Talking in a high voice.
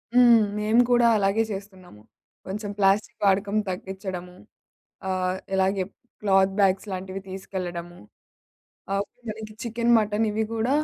Yes: high, 195 Hz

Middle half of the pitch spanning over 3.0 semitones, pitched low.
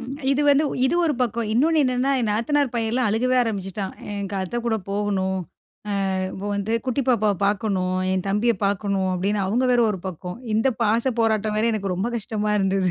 No: average, 3.5 semitones; high, 215 Hz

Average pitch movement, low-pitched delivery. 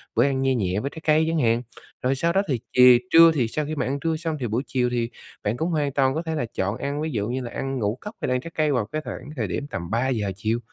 Yes: average, 4.7 semitones; low, 130 Hz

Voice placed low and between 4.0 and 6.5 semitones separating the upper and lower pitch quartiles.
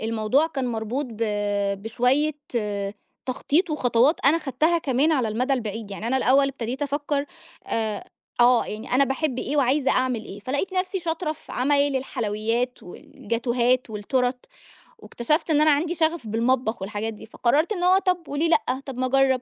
No: very high, 260 Hz; average, 4.4 semitones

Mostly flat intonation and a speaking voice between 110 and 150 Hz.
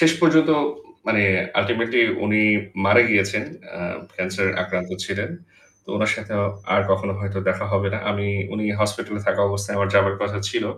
No: narrow, 1.7 semitones; low, 100 Hz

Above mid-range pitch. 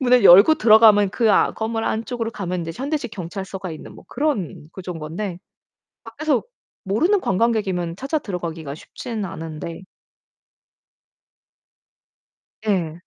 Yes: high, 200 Hz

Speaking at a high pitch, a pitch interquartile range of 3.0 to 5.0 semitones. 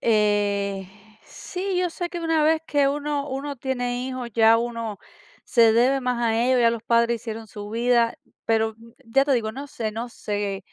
Yes: high, 235 Hz; average, 3.7 semitones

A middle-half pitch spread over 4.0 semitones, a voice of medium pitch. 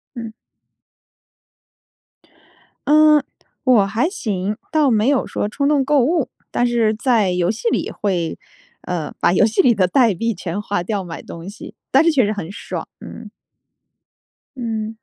No: average, 5.2 semitones; high, 220 Hz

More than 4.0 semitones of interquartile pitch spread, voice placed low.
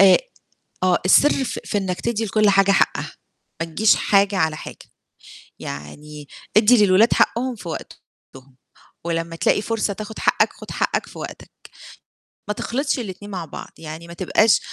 No: average, 4.5 semitones; high, 195 Hz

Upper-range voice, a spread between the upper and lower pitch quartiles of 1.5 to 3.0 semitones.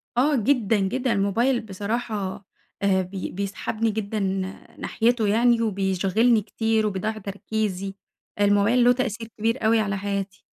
Yes: high, 215 Hz; narrow, 2.5 semitones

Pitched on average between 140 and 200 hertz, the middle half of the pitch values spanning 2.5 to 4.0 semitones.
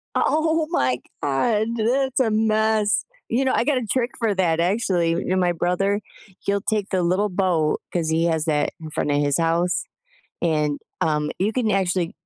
No: medium, 185 Hz; average, 5.0 semitones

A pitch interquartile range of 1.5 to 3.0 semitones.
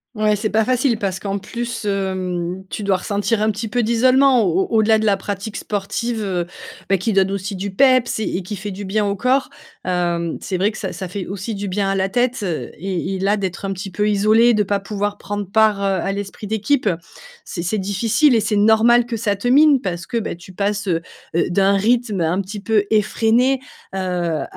Yes: narrow, 2.6 semitones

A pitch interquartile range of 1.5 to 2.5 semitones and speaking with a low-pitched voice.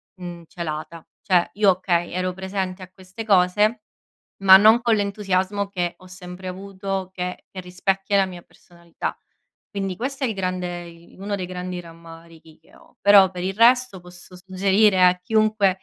No: narrow, 1.9 semitones; medium, 185 Hz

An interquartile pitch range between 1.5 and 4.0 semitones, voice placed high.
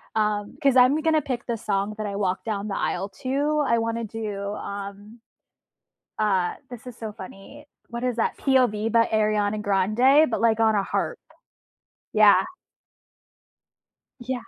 Yes: average, 3.3 semitones; high, 220 Hz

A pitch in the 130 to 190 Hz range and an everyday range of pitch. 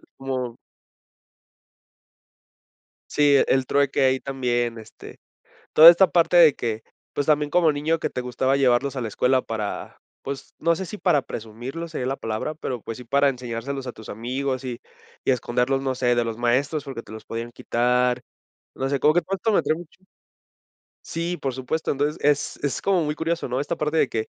Yes: low, 135 Hz; average, 3.7 semitones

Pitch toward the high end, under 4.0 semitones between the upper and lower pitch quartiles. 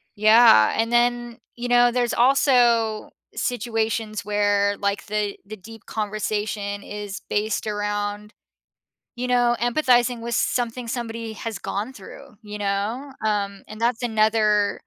Yes: high, 220 Hz; narrow, 2.6 semitones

